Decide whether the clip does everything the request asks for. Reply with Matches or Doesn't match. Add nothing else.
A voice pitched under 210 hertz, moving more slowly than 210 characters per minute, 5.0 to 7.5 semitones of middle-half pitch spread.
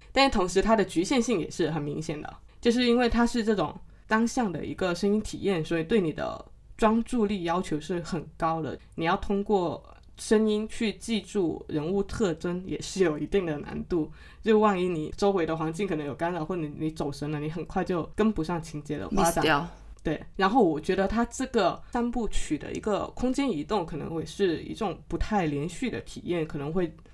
Doesn't match